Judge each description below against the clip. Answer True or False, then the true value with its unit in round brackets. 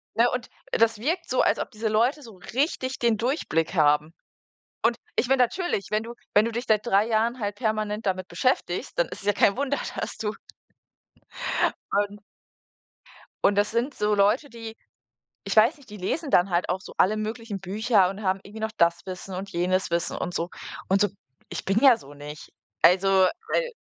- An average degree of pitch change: True (3.7 semitones)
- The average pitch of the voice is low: False (215 Hz)